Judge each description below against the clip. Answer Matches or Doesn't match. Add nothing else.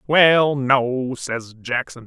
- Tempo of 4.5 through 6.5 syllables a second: Doesn't match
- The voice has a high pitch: Doesn't match